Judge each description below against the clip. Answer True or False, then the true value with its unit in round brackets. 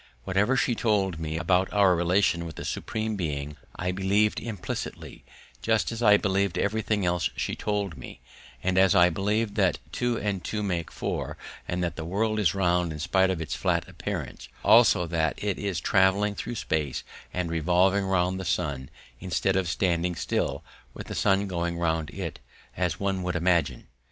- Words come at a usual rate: True (175 wpm)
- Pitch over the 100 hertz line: False (95 Hz)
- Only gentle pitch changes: False (3.0 semitones)